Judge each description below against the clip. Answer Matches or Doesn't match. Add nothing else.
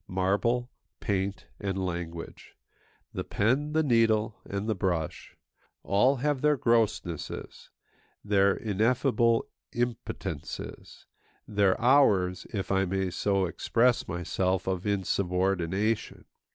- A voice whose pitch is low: Matches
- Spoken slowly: Matches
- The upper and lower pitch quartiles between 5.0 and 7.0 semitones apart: Doesn't match